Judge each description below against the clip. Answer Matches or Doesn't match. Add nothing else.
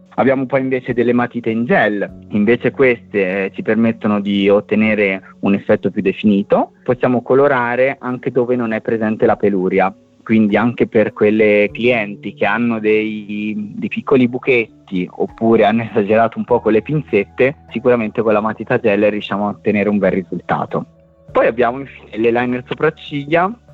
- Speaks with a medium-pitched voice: Doesn't match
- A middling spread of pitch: Matches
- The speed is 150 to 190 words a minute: Matches